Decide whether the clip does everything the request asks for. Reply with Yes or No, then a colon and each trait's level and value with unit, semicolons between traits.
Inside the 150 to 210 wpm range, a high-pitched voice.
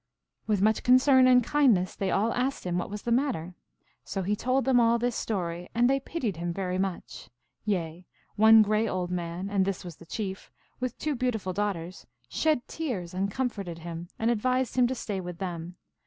Yes: average, 200 wpm; high, 205 Hz